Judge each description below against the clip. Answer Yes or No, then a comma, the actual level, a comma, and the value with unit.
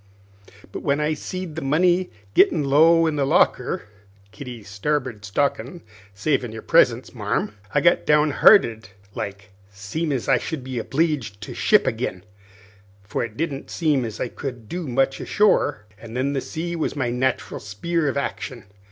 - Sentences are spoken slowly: No, average, 165 wpm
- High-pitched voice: No, low, 135 Hz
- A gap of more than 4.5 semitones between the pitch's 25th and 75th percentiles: Yes, wide, 5.6 semitones